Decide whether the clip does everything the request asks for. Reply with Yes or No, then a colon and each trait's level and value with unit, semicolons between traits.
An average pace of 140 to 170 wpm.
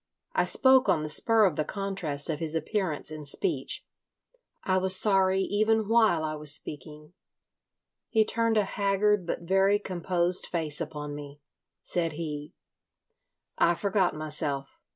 Yes: average, 145 wpm